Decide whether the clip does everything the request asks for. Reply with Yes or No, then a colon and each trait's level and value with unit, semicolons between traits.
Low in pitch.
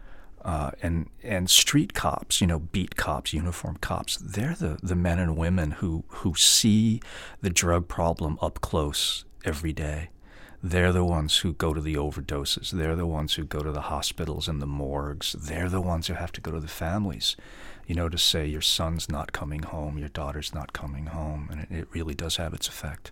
Yes: very low, 80 Hz